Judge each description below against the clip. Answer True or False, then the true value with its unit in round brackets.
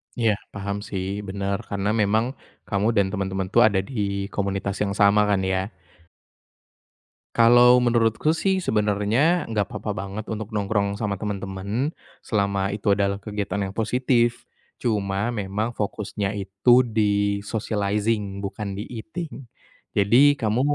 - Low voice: True (105 Hz)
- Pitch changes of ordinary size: False (2.2 semitones)